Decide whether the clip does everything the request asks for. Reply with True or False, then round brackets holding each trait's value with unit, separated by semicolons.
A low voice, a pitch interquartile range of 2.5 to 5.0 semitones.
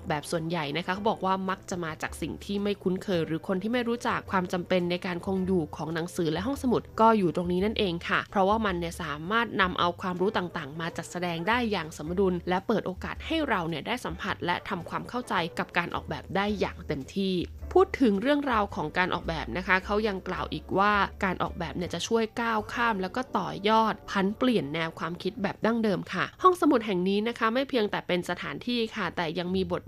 False (190 Hz; 4.0 semitones)